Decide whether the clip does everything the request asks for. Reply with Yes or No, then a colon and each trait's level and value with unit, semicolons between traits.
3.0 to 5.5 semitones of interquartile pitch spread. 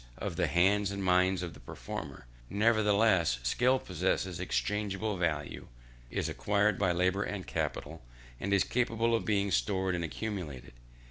No: narrow, 2.5 semitones